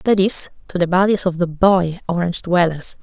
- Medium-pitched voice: Yes, medium, 180 Hz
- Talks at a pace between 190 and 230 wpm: Yes, average, 200 wpm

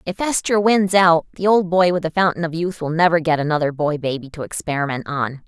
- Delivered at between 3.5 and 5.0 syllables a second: No, 5.8 syllables/s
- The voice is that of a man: No, female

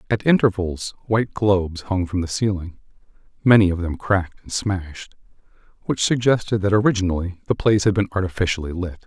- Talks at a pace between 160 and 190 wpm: No, average, 145 wpm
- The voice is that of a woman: No, male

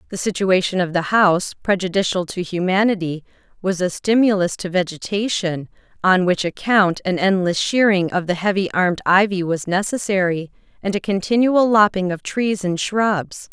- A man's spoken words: No, female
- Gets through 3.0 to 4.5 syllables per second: No, 5.0 syllables/s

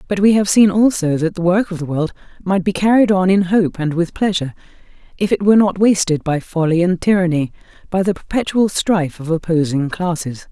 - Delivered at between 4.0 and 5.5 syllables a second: No, 5.7 syllables/s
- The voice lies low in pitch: No, medium, 180 Hz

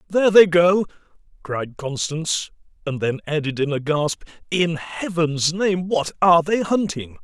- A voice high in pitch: No, medium, 165 Hz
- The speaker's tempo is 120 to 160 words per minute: Yes, average, 150 wpm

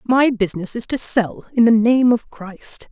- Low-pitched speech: No, high, 225 Hz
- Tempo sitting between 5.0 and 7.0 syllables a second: No, 4.4 syllables/s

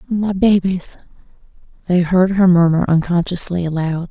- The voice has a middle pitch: Yes, medium, 180 Hz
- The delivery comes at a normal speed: No, slow, 115 wpm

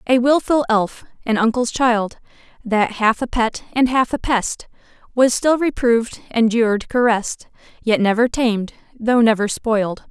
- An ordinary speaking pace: Yes, average, 145 wpm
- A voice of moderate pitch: No, high, 230 Hz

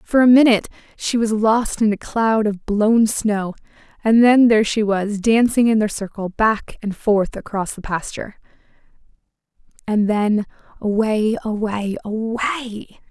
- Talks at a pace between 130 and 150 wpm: Yes, average, 145 wpm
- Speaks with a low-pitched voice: No, high, 215 Hz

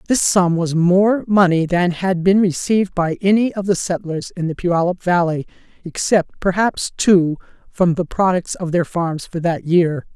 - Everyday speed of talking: Yes, average, 175 wpm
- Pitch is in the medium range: Yes, medium, 180 Hz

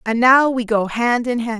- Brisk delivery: Yes, fast, 265 wpm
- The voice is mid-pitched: No, high, 235 Hz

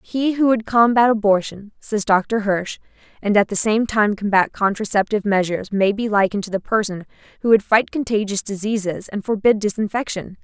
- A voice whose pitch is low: No, high, 210 Hz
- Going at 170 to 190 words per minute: Yes, average, 175 wpm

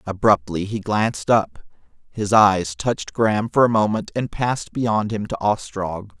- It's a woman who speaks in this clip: No, male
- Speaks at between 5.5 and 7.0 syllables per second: No, 4.6 syllables/s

